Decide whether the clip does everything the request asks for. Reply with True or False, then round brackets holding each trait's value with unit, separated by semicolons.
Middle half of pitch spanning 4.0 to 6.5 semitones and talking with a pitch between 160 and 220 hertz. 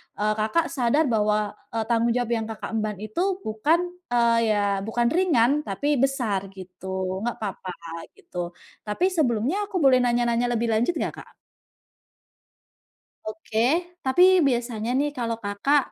False (4.4 semitones; 230 Hz)